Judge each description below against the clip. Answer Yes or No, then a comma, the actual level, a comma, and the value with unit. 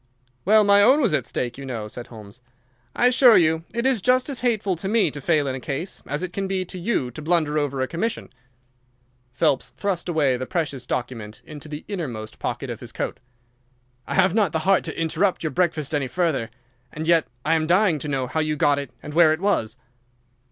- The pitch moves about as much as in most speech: No, wide, 6.0 semitones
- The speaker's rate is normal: No, fast, 220 wpm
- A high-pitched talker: No, medium, 160 Hz